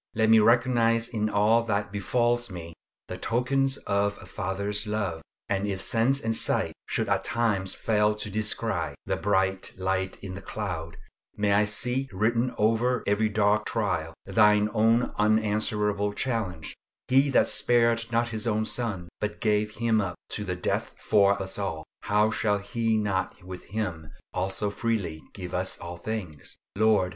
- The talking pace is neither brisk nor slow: Yes, average, 160 wpm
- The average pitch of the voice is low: Yes, low, 105 Hz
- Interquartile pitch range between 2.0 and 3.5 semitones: Yes, average, 2.8 semitones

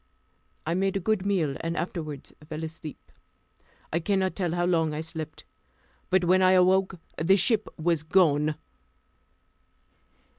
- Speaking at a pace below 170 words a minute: Yes, average, 140 wpm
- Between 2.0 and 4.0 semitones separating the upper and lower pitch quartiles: Yes, average, 2.9 semitones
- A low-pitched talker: No, medium, 175 Hz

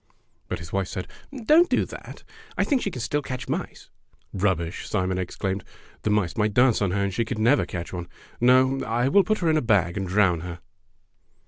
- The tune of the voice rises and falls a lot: Yes, wide, 5.9 semitones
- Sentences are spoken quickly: Yes, fast, 230 wpm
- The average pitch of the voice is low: Yes, low, 105 Hz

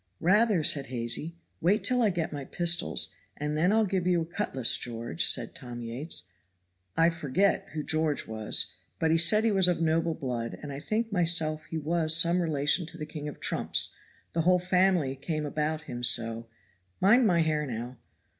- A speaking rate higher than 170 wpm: Yes, average, 185 wpm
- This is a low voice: No, medium, 160 Hz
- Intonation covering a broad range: No, average, 4.1 semitones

